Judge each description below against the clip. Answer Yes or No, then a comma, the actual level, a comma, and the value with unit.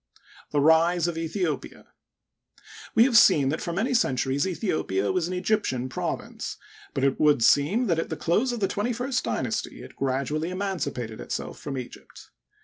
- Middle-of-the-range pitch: Yes, medium, 165 Hz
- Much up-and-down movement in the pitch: Yes, wide, 6.5 semitones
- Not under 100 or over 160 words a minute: No, average, 170 wpm